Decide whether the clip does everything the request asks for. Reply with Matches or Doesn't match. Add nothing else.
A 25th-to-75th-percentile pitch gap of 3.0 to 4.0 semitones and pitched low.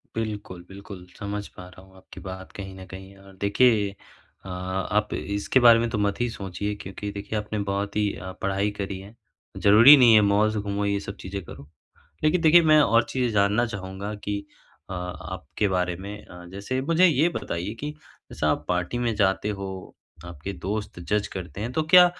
Doesn't match